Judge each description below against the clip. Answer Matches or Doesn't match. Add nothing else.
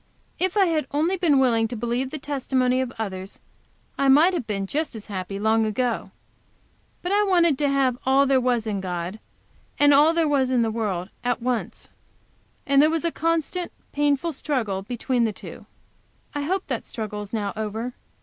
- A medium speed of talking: Matches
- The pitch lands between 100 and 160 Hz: Doesn't match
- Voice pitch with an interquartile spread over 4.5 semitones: Matches